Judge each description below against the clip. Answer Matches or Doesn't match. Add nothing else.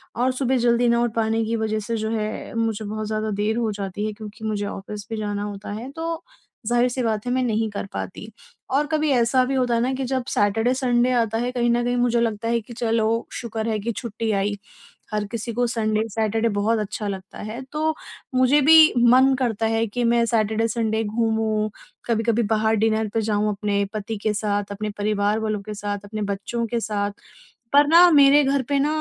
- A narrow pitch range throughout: Matches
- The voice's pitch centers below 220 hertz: Doesn't match